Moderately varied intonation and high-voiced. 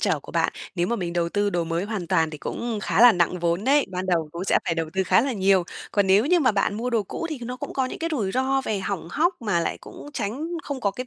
No: wide, 6.2 semitones; high, 205 Hz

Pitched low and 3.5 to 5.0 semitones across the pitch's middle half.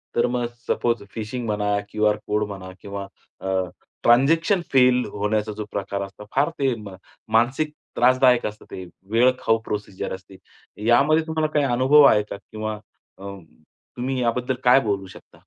Yes: low, 115 Hz; average, 3.8 semitones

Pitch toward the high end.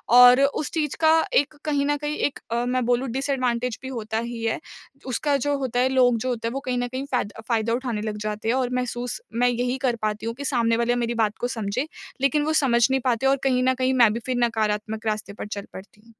Yes: high, 245 Hz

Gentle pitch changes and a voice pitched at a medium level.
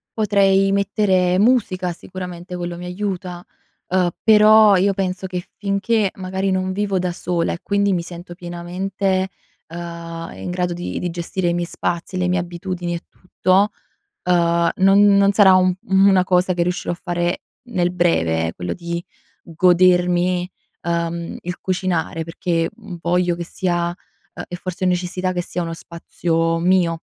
Yes: narrow, 1.6 semitones; medium, 180 Hz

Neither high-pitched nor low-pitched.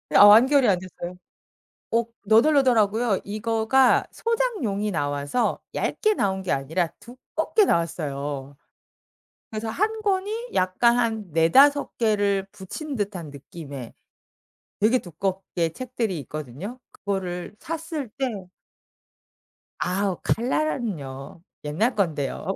No: high, 205 Hz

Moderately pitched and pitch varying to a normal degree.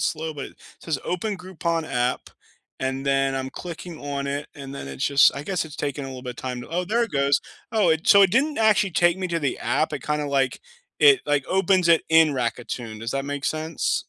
Yes: medium, 150 Hz; average, 4.6 semitones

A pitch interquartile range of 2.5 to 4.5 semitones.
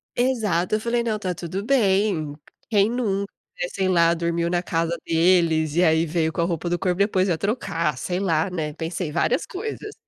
Yes: average, 3.5 semitones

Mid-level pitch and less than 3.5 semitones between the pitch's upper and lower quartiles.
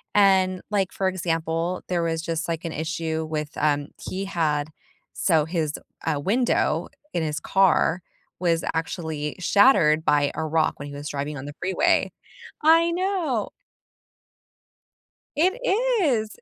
No: medium, 165 Hz; average, 3.9 semitones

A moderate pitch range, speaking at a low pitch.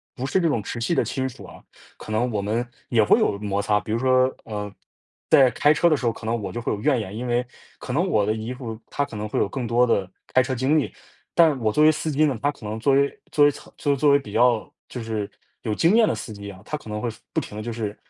Yes: average, 4.6 semitones; low, 120 Hz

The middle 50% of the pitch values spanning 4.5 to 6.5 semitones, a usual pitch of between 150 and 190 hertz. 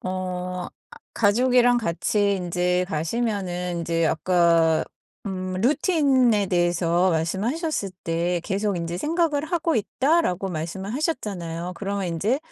Yes: wide, 5.4 semitones; medium, 185 Hz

